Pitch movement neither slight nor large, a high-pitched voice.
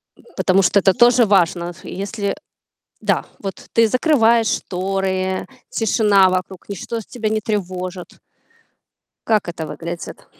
Yes: average, 3.0 semitones; high, 195 Hz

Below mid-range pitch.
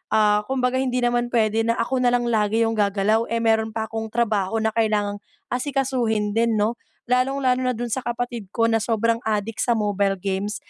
No: high, 225 Hz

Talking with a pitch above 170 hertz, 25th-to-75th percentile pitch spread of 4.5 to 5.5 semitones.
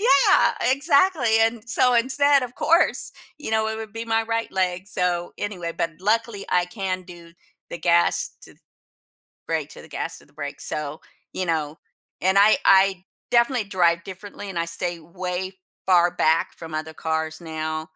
Yes: medium, 185 Hz; average, 4.9 semitones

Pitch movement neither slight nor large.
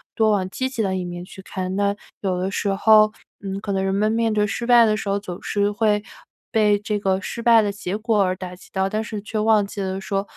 No: narrow, 2.0 semitones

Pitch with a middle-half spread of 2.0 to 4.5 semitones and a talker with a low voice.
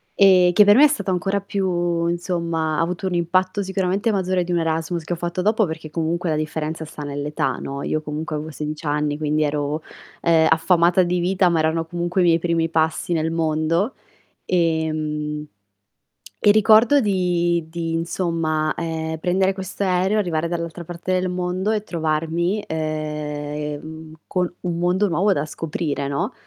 No: narrow, 2.6 semitones; medium, 170 Hz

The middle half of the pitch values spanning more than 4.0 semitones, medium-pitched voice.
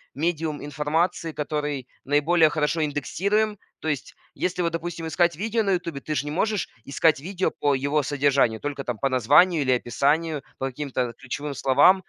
No: average, 3.4 semitones; medium, 150 Hz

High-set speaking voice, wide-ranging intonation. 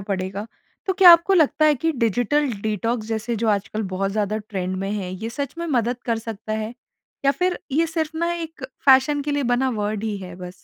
Yes: high, 230 Hz; wide, 5.9 semitones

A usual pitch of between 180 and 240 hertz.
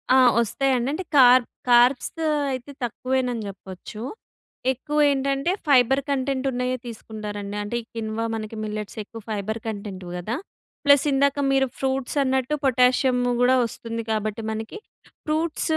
No: very high, 250 Hz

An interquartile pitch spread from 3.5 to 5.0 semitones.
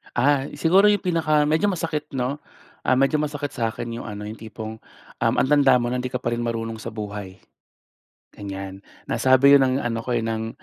Yes: average, 4.6 semitones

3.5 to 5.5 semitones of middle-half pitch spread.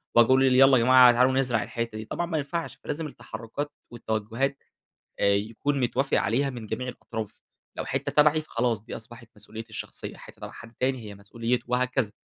No: average, 3.1 semitones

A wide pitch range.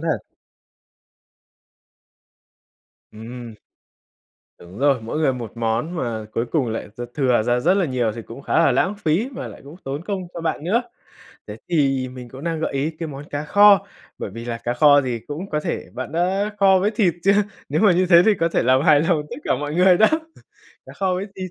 Yes: wide, 6.7 semitones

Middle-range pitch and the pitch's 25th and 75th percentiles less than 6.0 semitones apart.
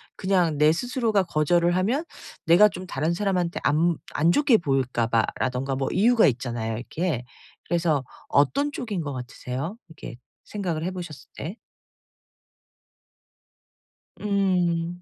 Yes: medium, 170 Hz; wide, 5.4 semitones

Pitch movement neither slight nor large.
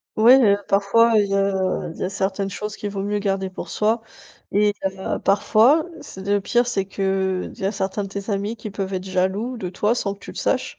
No: narrow, 1.7 semitones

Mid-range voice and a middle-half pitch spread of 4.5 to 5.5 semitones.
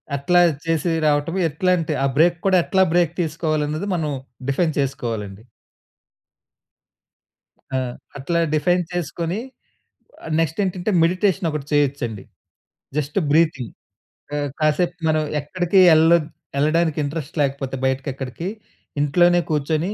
No: medium, 155 Hz; average, 3.5 semitones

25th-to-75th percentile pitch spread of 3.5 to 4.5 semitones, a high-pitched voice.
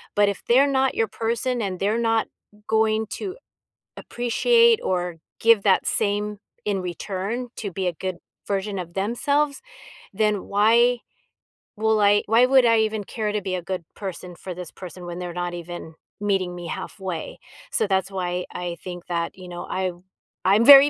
Yes: average, 3.9 semitones; high, 205 Hz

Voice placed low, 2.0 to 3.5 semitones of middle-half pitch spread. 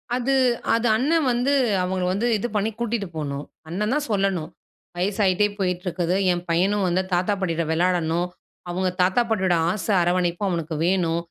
No: medium, 185 Hz; average, 3.2 semitones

